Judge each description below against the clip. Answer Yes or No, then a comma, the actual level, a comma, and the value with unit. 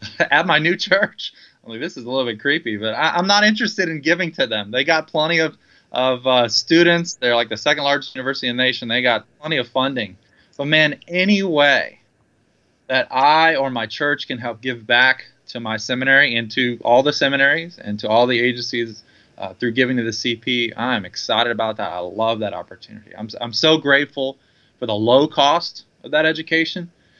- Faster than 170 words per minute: Yes, fast, 205 wpm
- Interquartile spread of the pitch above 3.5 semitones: Yes, average, 4.8 semitones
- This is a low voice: Yes, low, 130 Hz